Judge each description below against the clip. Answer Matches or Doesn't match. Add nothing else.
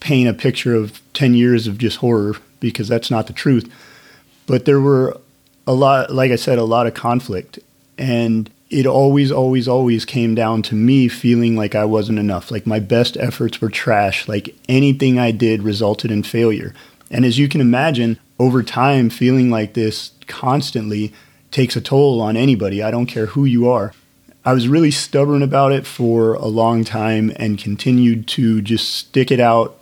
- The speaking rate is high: Doesn't match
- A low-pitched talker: Matches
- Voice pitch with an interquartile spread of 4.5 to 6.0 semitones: Doesn't match